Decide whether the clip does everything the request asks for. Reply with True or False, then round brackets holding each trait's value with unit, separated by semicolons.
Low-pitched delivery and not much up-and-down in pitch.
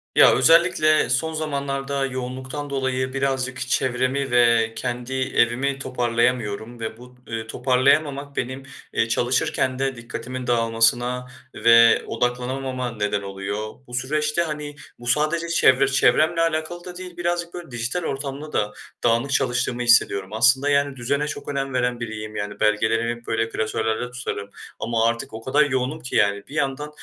False (130 Hz; 3.1 semitones)